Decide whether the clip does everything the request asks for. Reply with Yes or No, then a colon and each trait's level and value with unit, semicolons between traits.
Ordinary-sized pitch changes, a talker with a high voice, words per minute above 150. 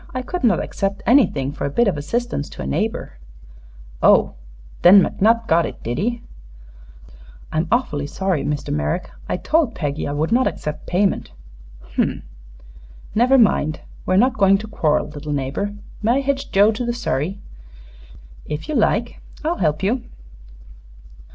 No: wide, 7.9 semitones; high, 195 Hz; average, 160 wpm